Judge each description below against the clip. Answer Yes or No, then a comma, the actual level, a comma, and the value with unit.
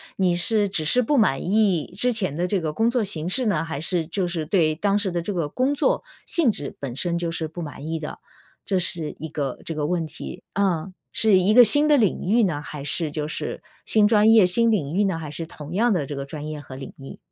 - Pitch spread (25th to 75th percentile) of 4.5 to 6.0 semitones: Yes, average, 5.2 semitones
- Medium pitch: Yes, medium, 175 Hz